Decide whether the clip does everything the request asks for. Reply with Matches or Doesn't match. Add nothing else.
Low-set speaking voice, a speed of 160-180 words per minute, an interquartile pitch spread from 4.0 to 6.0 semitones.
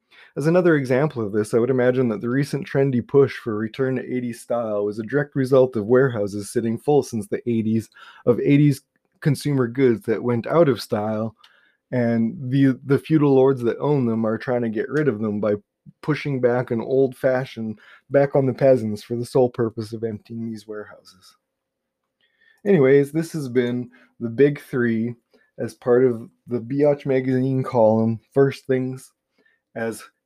Doesn't match